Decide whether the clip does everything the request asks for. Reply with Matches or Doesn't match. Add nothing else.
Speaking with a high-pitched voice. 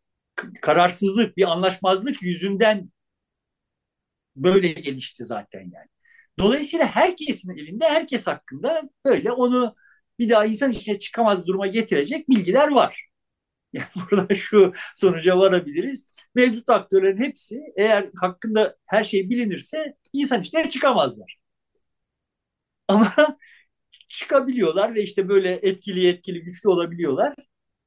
Matches